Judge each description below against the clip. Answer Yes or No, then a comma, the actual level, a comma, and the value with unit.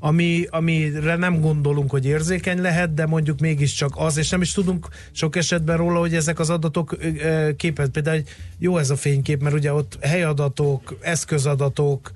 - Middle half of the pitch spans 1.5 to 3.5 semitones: Yes, average, 2.7 semitones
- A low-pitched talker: No, medium, 160 Hz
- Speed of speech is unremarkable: No, fast, 165 wpm